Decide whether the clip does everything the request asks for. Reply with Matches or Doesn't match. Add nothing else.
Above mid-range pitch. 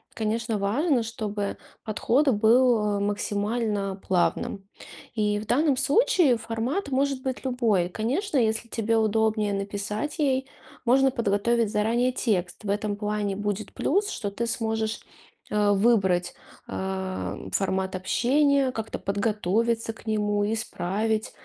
Matches